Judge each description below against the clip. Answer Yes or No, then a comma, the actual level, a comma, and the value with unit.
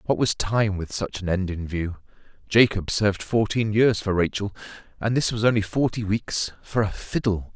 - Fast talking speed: No, average, 190 wpm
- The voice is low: Yes, low, 105 Hz